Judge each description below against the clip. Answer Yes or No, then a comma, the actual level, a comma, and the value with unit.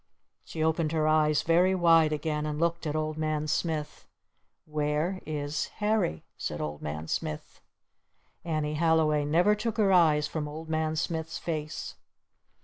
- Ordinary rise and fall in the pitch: No, narrow, 1.7 semitones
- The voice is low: No, medium, 155 Hz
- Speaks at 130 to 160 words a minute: Yes, average, 145 wpm